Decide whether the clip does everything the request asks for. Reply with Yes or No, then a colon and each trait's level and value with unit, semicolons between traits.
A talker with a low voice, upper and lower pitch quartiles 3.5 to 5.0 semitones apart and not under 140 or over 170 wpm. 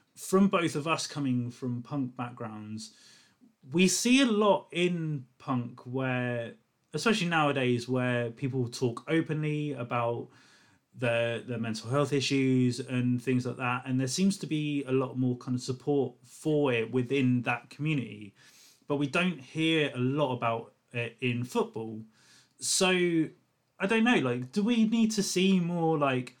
Yes: low, 130 Hz; average, 4.5 semitones; average, 155 wpm